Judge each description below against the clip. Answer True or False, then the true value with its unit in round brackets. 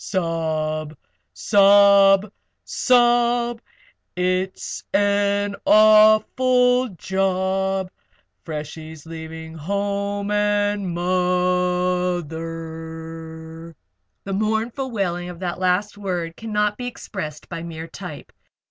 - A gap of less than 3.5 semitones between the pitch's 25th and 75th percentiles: False (3.9 semitones)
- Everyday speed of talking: False (85 wpm)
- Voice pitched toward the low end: False (190 Hz)